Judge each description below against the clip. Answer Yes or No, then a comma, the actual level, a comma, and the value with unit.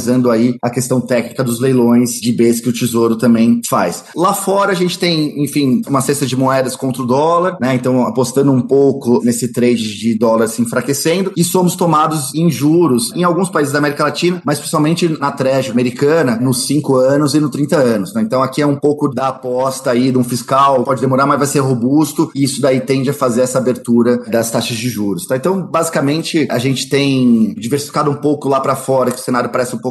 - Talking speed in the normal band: No, fast, 215 wpm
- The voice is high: No, low, 135 Hz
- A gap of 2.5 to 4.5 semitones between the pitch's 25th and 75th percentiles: Yes, average, 3.1 semitones